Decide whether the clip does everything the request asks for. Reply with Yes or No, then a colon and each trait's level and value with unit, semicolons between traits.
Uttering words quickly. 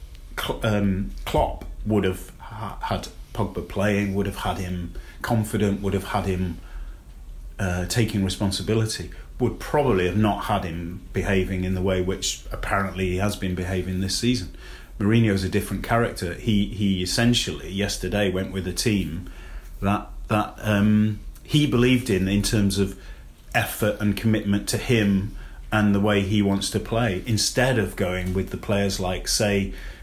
No: average, 160 wpm